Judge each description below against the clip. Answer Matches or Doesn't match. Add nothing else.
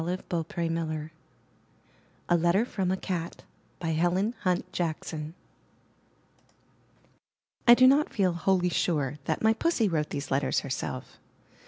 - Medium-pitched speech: Matches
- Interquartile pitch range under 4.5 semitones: Matches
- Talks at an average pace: Doesn't match